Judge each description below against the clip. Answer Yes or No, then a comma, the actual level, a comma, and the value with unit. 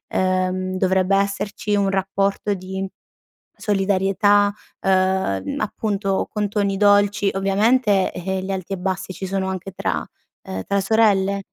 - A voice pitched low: No, high, 195 Hz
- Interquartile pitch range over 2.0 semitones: No, narrow, 1.4 semitones